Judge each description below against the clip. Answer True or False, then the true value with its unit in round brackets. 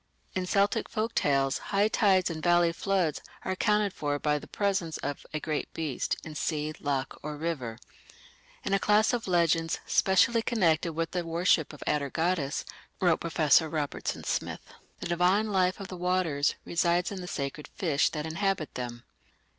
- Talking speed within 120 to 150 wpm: False (165 wpm)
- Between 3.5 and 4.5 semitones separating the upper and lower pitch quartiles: True (3.8 semitones)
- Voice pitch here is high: False (170 Hz)